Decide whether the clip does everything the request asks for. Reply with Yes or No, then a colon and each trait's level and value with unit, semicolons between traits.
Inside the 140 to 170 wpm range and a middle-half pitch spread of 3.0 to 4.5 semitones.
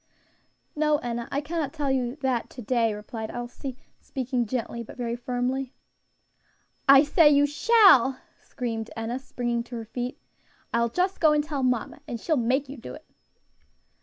Yes: average, 165 wpm; average, 3.3 semitones